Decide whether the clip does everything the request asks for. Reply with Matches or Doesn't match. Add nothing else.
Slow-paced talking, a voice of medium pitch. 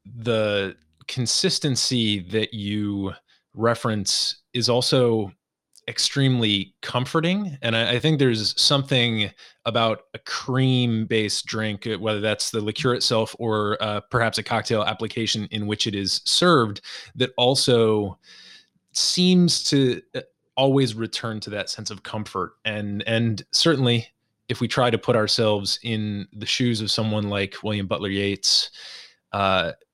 Doesn't match